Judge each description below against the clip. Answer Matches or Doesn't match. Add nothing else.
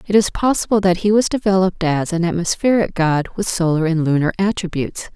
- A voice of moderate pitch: Matches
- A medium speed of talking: Matches